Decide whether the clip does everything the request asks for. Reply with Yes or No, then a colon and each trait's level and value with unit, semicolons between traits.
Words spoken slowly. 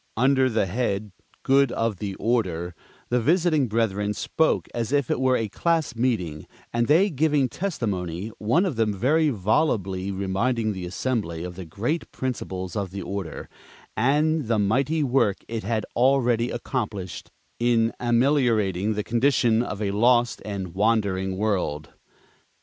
No: average, 145 wpm